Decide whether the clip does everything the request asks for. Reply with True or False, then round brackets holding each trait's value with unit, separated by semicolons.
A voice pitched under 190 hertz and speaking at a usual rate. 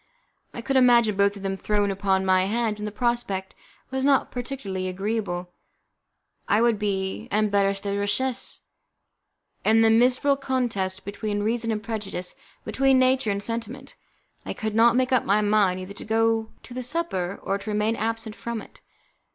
False (215 Hz; 170 wpm)